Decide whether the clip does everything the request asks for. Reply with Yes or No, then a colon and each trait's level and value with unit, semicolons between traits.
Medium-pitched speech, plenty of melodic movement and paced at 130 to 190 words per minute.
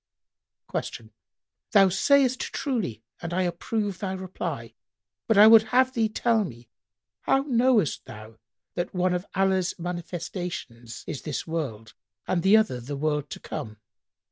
Yes: medium, 180 Hz; wide, 6.8 semitones; average, 145 wpm